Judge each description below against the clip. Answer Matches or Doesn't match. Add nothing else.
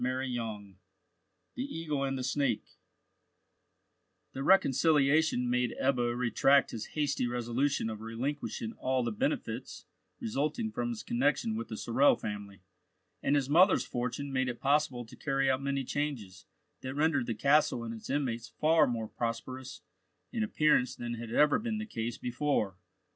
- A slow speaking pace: Doesn't match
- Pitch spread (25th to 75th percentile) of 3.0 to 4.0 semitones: Matches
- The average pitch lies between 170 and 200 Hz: Doesn't match